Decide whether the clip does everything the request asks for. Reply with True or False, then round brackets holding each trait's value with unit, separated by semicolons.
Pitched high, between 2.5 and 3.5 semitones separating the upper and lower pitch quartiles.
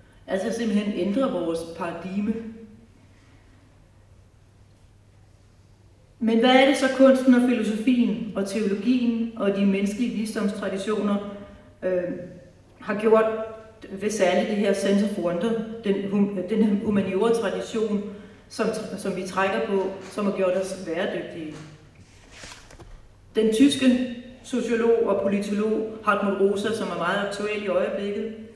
False (200 Hz; 3.9 semitones)